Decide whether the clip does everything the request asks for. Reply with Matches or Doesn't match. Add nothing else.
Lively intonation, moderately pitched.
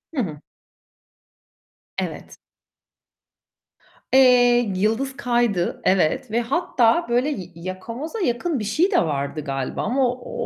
Doesn't match